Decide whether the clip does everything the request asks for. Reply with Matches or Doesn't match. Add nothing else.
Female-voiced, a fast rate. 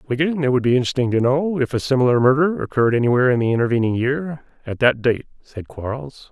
Doesn't match